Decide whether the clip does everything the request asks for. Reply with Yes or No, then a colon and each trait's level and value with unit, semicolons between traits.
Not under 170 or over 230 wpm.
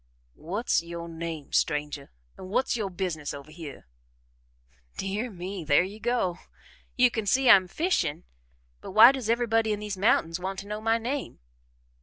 No: average, 160 wpm